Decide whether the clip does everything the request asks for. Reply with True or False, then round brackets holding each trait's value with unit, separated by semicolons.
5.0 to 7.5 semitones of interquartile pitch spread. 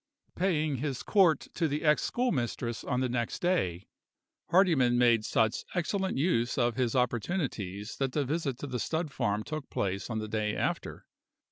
True (5.6 semitones)